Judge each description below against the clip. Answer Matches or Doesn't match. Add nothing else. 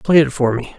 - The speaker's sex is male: Matches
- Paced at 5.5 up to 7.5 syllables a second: Matches